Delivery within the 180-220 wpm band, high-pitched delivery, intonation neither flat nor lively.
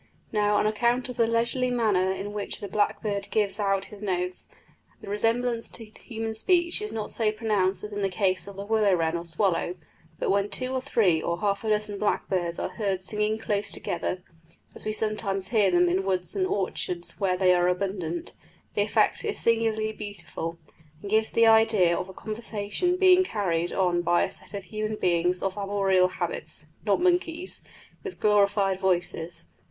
Yes: average, 185 wpm; high, 205 Hz; average, 3.2 semitones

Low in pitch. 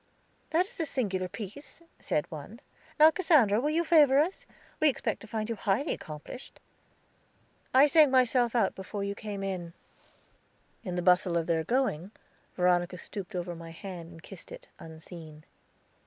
No: high, 200 Hz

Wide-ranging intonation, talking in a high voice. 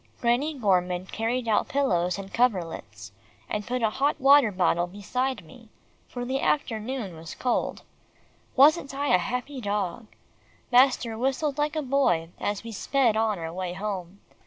Yes: wide, 6.1 semitones; high, 225 Hz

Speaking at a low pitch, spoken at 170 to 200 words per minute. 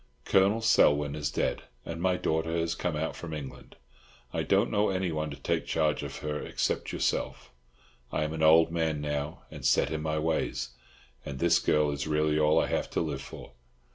Yes: very low, 80 Hz; average, 195 wpm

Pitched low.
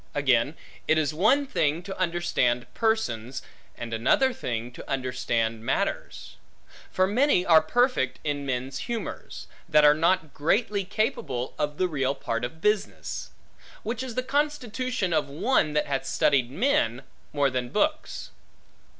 No: medium, 155 Hz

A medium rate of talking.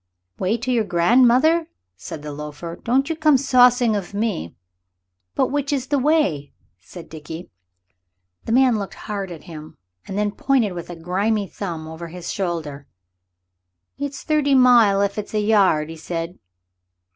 Yes: average, 155 wpm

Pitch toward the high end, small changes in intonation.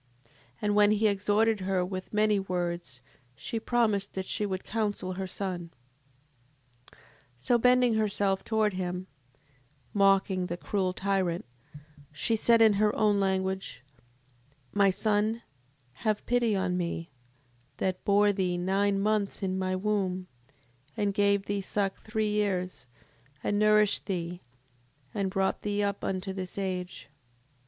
Yes: high, 195 Hz; narrow, 2.1 semitones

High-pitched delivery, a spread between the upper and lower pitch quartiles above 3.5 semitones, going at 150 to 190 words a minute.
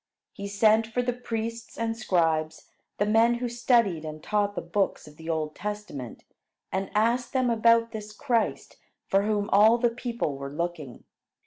Yes: high, 210 Hz; average, 5.2 semitones; average, 165 wpm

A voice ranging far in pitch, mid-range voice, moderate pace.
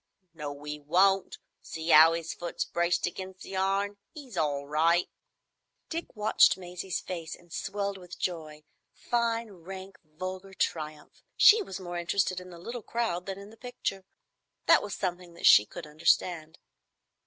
No: average, 3.2 semitones; medium, 180 Hz; average, 155 wpm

